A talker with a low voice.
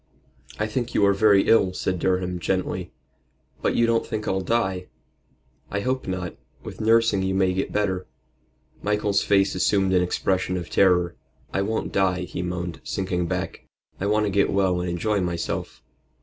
Yes: very low, 95 Hz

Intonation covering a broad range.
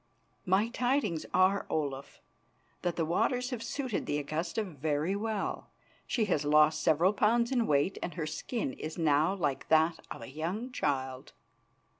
Yes: wide, 6.2 semitones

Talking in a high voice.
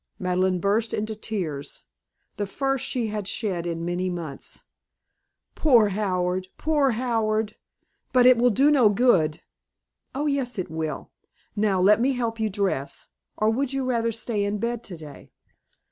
Yes: high, 215 Hz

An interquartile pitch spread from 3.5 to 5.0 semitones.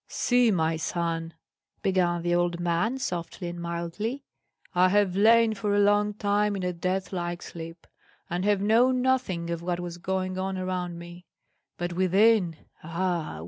No: average, 3.1 semitones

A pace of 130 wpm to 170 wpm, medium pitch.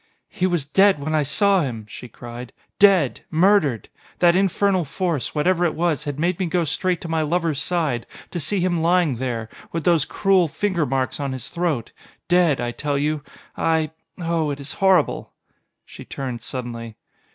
No: average, 180 wpm; medium, 160 Hz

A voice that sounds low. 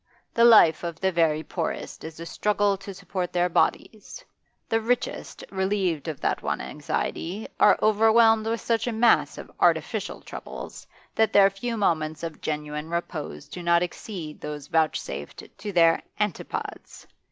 No: medium, 180 Hz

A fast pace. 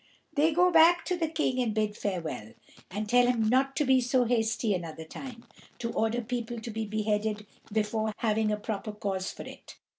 No: average, 190 wpm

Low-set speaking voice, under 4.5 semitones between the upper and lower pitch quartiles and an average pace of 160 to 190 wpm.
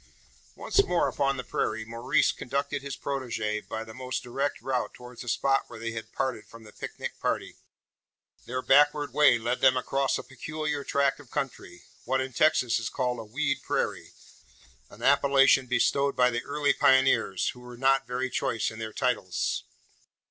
Yes: low, 130 Hz; average, 2.8 semitones; average, 175 wpm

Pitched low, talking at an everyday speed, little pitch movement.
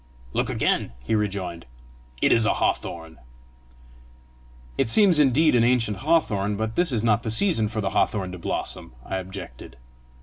No: low, 110 Hz; average, 160 wpm; average, 4.5 semitones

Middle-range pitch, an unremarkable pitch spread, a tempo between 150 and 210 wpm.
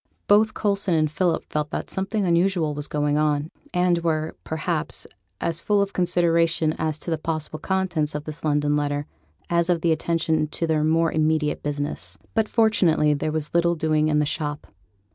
No: medium, 160 Hz; narrow, 2.3 semitones; average, 175 wpm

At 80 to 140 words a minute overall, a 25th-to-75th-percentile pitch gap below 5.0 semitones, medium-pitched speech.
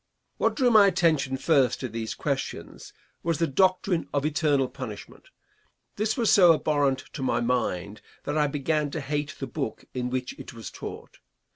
No: average, 170 wpm; average, 4.1 semitones; medium, 145 Hz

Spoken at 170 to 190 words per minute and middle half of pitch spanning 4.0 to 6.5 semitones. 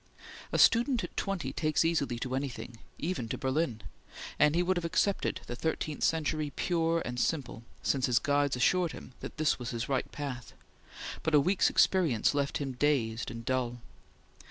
Yes: average, 175 wpm; average, 4.8 semitones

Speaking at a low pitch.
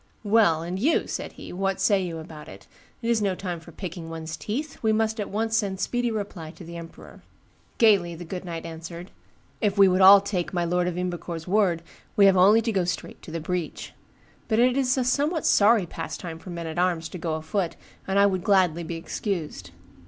No: medium, 185 Hz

